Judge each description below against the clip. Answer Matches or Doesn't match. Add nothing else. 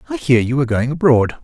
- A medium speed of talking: Doesn't match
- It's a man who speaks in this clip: Matches